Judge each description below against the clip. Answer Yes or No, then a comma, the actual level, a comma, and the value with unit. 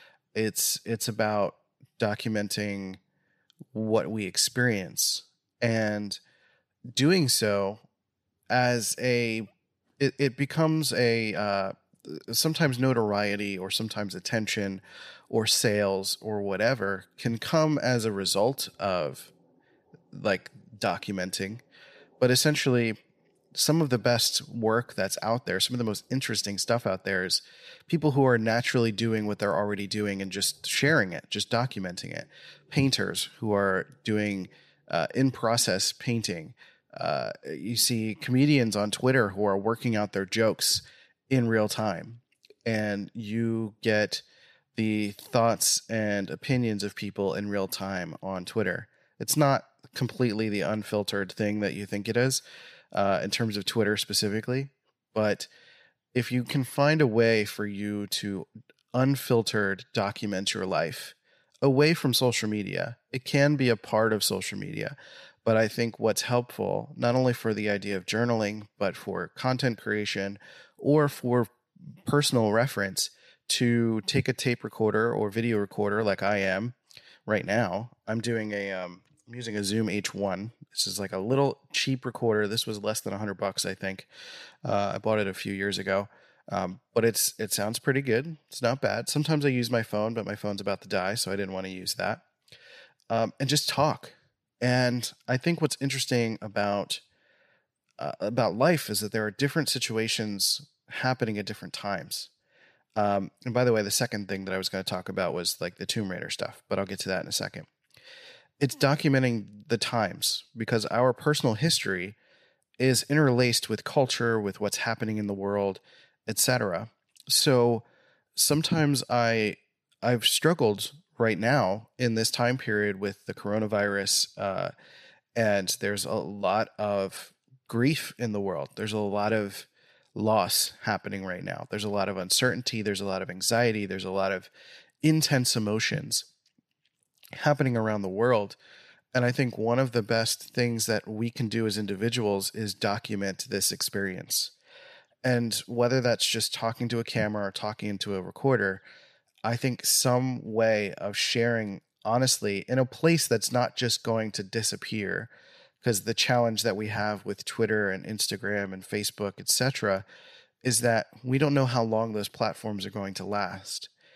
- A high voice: No, low, 110 Hz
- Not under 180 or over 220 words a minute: No, average, 160 wpm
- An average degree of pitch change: Yes, average, 3.4 semitones